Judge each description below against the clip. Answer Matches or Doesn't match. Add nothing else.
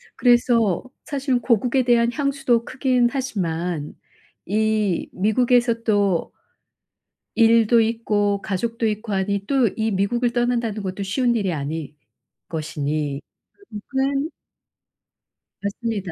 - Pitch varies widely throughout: Doesn't match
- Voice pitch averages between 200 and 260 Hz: Matches